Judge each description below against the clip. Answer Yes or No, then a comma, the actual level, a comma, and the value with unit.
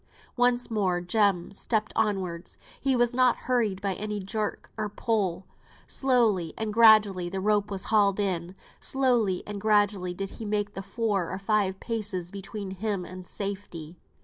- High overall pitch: Yes, high, 205 Hz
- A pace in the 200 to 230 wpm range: No, average, 155 wpm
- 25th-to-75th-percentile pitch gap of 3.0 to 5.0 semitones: No, narrow, 2.6 semitones